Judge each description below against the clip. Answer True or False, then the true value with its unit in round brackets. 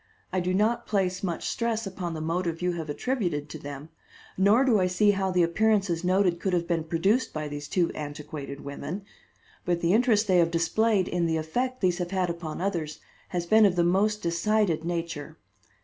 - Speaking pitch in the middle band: True (180 Hz)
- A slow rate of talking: False (195 wpm)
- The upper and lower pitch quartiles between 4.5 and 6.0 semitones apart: False (3.4 semitones)